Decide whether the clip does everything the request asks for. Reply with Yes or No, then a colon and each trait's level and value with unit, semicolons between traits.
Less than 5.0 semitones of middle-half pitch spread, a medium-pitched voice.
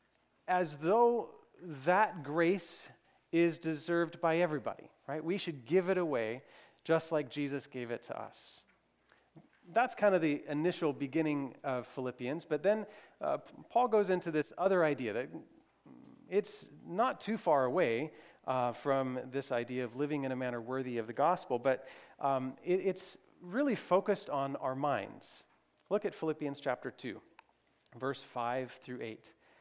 No: wide, 5.4 semitones; medium, 155 Hz